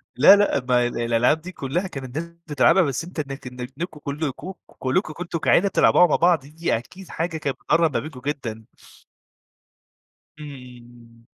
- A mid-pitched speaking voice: Yes, medium, 145 Hz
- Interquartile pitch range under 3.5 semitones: No, average, 5.0 semitones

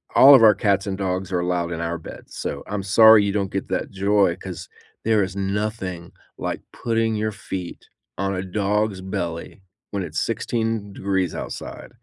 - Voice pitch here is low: Yes, very low, 95 Hz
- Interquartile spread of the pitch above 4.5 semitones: No, narrow, 2.4 semitones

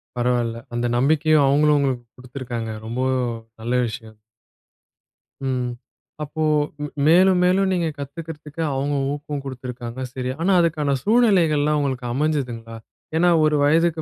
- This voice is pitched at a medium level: Yes, medium, 145 Hz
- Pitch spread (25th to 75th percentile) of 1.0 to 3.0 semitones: No, average, 4.1 semitones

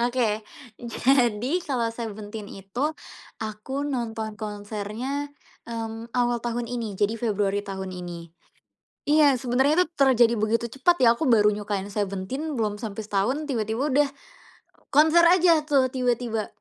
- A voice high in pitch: Yes, high, 230 Hz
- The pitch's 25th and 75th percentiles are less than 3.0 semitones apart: No, average, 4.0 semitones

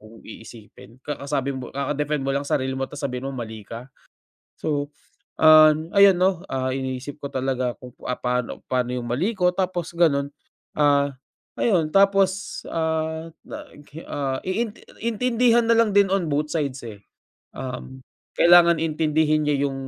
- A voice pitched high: No, medium, 145 Hz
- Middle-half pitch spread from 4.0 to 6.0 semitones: Yes, average, 4.8 semitones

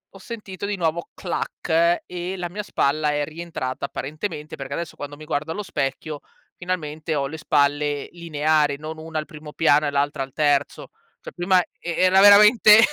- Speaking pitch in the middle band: Yes, medium, 155 Hz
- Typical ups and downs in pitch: Yes, average, 3.5 semitones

